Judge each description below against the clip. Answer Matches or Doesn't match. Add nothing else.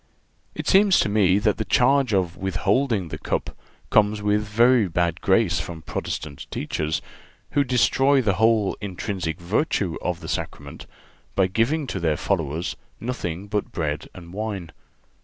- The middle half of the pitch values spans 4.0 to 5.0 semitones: Matches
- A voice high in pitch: Doesn't match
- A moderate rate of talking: Matches